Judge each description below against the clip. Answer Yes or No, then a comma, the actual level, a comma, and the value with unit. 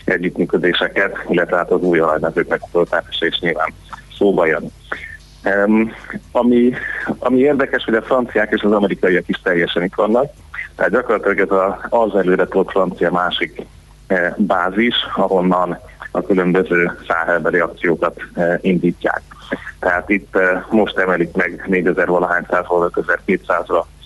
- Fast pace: No, average, 110 wpm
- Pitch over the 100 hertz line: No, very low, 95 Hz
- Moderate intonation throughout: Yes, average, 3.5 semitones